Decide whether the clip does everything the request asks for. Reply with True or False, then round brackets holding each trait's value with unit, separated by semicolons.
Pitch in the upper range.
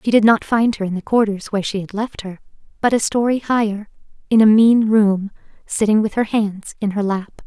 True (215 Hz)